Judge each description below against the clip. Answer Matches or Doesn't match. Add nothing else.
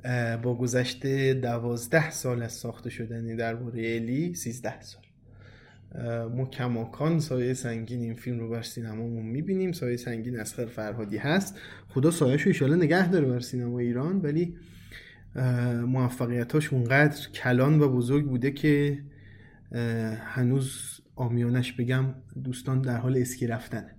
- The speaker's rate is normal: Matches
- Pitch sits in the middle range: Doesn't match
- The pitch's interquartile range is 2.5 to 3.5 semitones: Matches